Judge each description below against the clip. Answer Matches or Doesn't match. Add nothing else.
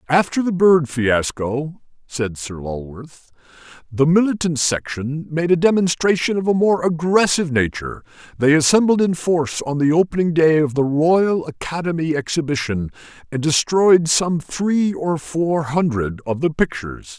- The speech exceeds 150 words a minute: Doesn't match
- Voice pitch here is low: Doesn't match